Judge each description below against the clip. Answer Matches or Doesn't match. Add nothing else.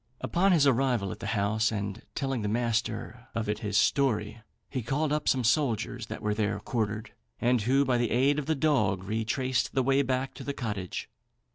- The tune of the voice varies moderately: Matches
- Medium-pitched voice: Doesn't match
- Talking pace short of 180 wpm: Doesn't match